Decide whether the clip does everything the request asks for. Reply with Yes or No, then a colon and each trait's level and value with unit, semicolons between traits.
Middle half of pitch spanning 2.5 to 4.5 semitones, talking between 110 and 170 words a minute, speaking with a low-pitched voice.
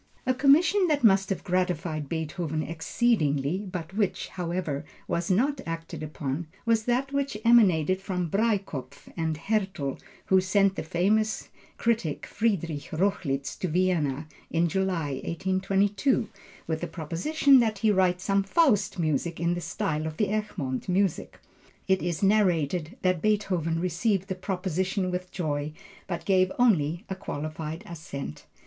No: average, 4.1 semitones; average, 140 wpm; medium, 185 Hz